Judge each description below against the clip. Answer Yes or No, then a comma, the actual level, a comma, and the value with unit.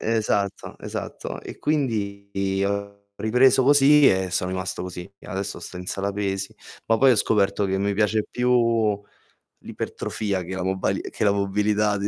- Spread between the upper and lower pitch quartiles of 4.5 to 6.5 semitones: No, narrow, 2.4 semitones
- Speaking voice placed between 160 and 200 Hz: No, low, 100 Hz